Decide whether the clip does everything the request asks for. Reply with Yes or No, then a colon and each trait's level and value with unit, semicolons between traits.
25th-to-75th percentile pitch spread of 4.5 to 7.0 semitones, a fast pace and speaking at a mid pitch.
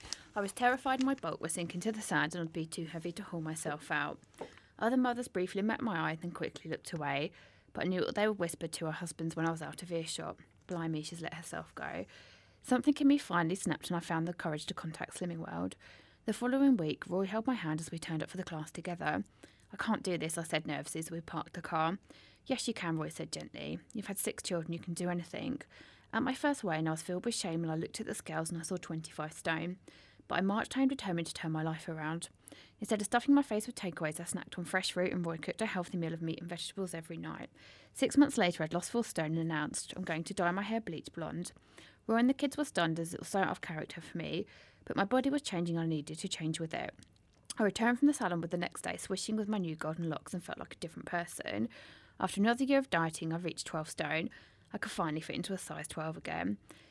Yes: average, 4.9 semitones; fast, 255 wpm; medium, 175 Hz